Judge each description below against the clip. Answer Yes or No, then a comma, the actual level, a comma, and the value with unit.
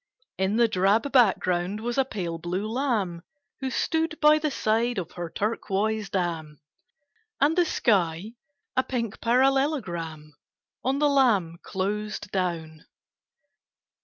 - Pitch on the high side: Yes, high, 210 Hz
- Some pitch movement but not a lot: No, wide, 6.7 semitones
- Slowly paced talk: Yes, slow, 125 wpm